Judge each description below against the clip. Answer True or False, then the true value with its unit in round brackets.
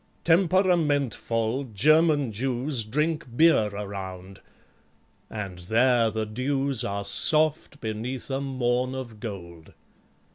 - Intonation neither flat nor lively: True (5.0 semitones)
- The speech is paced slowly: True (100 wpm)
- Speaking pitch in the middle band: False (125 Hz)